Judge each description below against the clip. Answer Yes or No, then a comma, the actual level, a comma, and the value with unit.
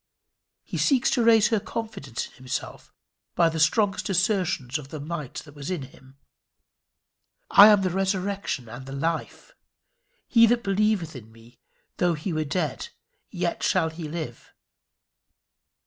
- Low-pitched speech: No, medium, 170 Hz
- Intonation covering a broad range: Yes, wide, 6.1 semitones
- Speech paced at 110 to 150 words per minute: Yes, average, 145 wpm